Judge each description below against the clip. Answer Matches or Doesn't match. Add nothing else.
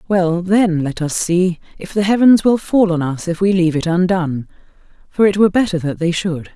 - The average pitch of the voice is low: Doesn't match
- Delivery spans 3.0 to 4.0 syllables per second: Doesn't match